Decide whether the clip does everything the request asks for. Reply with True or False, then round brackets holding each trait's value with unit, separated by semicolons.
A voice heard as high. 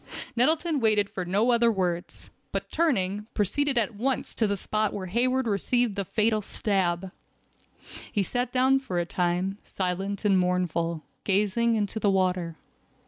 True (205 Hz)